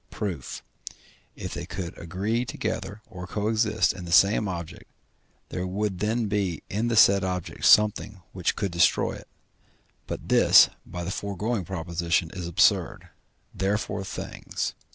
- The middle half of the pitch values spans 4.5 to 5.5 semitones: No, average, 3.1 semitones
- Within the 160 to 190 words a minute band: No, average, 150 wpm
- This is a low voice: Yes, very low, 95 Hz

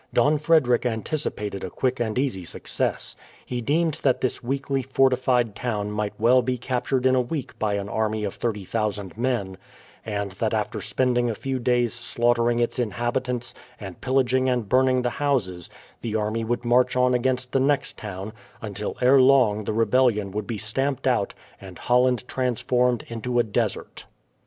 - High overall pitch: No, low, 120 Hz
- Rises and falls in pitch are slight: No, average, 3.2 semitones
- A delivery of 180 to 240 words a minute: No, average, 165 wpm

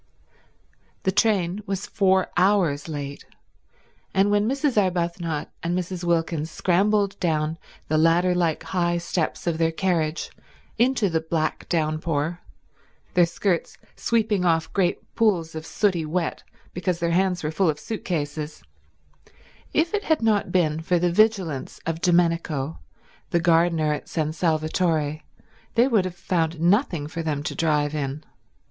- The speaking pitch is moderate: Yes, medium, 170 Hz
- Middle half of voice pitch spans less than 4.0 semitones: Yes, average, 3.1 semitones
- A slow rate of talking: No, average, 145 wpm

